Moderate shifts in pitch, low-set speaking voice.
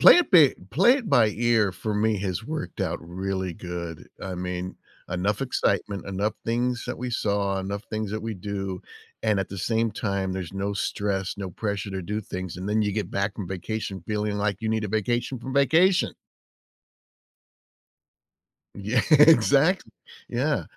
Yes: average, 3.1 semitones; low, 105 Hz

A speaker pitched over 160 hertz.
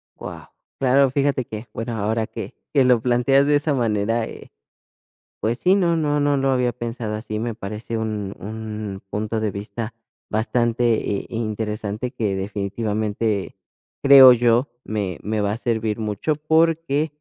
No: low, 115 Hz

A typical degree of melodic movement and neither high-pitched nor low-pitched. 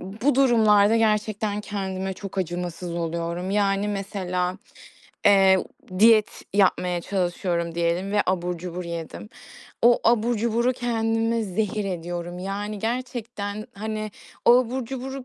No: average, 3.8 semitones; high, 200 Hz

